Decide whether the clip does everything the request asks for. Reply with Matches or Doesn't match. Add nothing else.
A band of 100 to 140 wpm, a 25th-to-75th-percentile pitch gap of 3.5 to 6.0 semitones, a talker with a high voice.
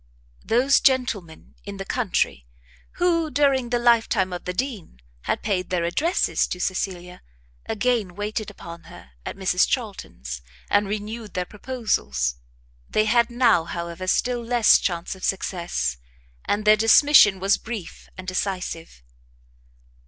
Matches